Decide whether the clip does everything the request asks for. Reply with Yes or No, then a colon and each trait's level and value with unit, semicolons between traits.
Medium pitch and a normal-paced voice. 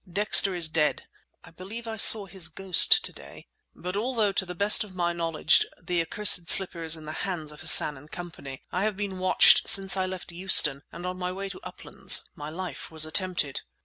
No: medium, 180 Hz; fast, 210 wpm